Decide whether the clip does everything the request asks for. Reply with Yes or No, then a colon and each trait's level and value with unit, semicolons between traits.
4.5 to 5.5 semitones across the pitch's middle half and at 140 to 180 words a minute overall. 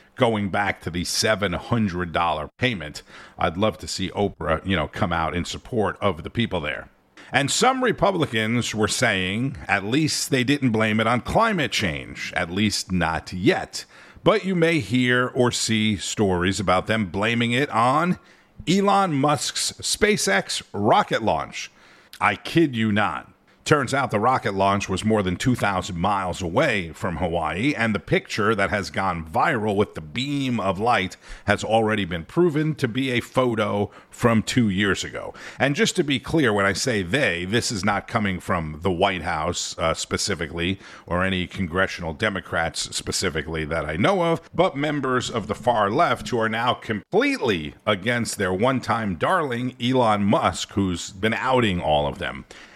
Yes: average, 5.1 semitones; average, 170 wpm